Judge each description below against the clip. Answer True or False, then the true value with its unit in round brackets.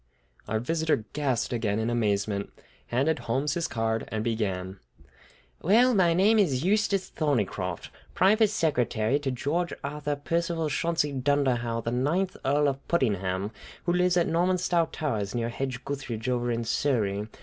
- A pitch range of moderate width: False (6.7 semitones)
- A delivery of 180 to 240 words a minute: False (145 wpm)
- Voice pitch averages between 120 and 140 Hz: True (135 Hz)